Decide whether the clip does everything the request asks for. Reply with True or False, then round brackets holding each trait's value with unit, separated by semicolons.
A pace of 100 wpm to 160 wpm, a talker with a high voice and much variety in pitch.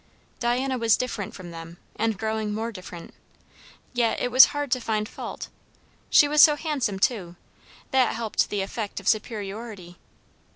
False (155 wpm; 220 Hz; 3.8 semitones)